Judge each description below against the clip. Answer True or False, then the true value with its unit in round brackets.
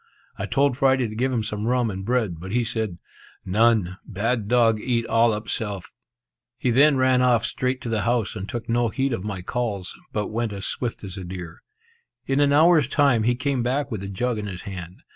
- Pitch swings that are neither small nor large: True (3.6 semitones)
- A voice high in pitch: False (115 Hz)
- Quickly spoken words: True (220 wpm)